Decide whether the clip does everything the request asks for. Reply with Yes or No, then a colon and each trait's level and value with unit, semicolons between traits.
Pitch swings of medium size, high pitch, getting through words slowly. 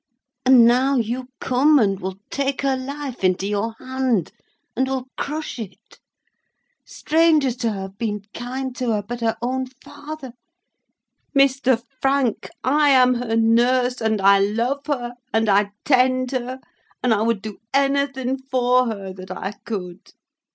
No: average, 3.2 semitones; very high, 250 Hz; average, 150 wpm